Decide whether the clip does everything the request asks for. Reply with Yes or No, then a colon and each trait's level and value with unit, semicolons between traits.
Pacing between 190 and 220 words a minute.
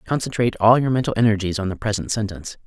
Yes: fast, 205 wpm